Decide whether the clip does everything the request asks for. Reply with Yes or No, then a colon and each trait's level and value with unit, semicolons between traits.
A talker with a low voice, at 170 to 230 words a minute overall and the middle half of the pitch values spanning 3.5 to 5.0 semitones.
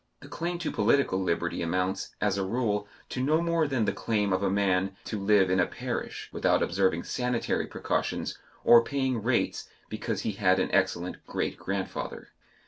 Yes: low, 100 Hz; average, 175 wpm; average, 4.7 semitones